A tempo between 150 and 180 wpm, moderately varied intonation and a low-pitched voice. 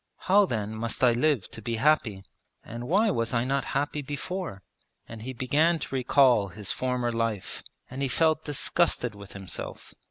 Yes: average, 170 wpm; average, 4.6 semitones; low, 125 Hz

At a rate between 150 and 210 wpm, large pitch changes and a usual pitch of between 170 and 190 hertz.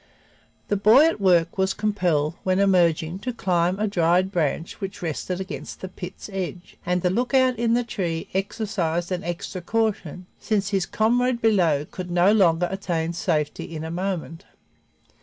No: average, 160 wpm; average, 3.3 semitones; medium, 185 Hz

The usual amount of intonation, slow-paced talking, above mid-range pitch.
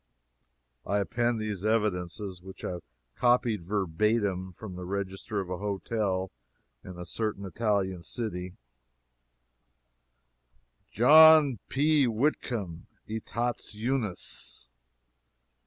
No: average, 3.9 semitones; slow, 90 wpm; low, 105 Hz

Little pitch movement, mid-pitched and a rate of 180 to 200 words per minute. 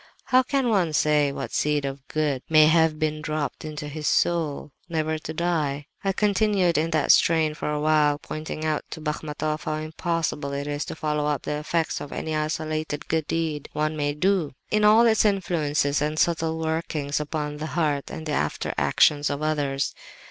Yes: narrow, 1.6 semitones; medium, 155 Hz; average, 185 wpm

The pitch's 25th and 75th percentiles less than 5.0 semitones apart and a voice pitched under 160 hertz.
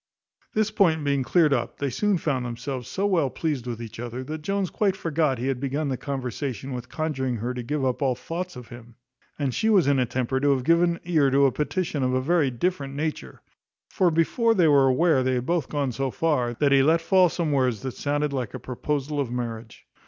Yes: average, 4.3 semitones; medium, 140 Hz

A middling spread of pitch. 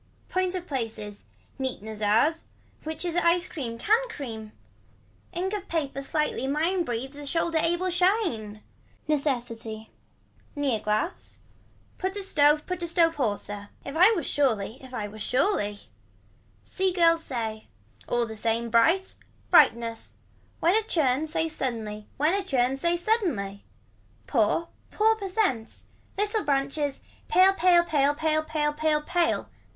No: wide, 7.1 semitones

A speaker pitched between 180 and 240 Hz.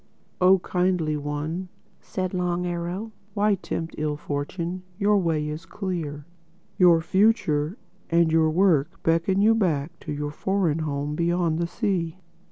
No: medium, 170 Hz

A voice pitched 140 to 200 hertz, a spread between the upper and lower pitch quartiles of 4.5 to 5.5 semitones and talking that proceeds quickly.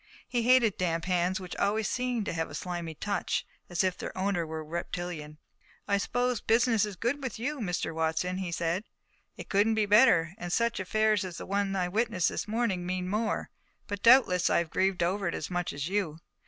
No: high, 190 Hz; average, 3.9 semitones; fast, 210 wpm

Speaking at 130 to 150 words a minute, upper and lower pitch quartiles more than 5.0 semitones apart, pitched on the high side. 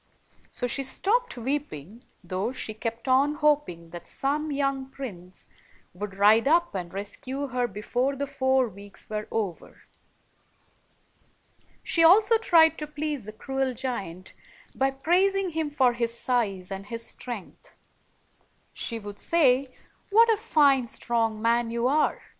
Yes: average, 140 wpm; wide, 5.5 semitones; very high, 255 Hz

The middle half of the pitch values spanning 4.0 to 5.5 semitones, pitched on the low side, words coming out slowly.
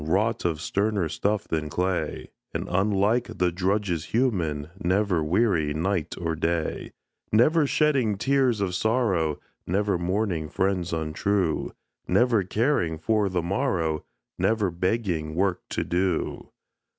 Yes: average, 4.3 semitones; very low, 95 Hz; slow, 125 wpm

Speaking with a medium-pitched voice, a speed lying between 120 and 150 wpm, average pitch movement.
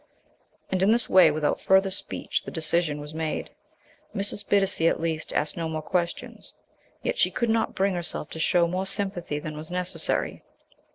No: medium, 175 Hz; average, 175 wpm; average, 3.4 semitones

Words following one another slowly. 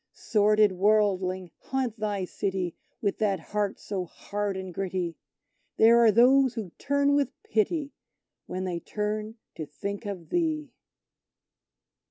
Yes: slow, 130 wpm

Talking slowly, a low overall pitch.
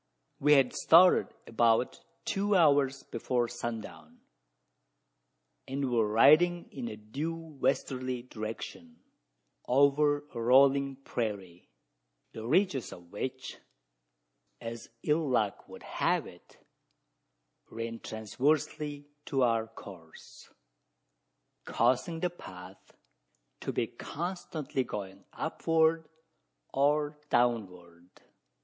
Yes: slow, 95 wpm; low, 130 Hz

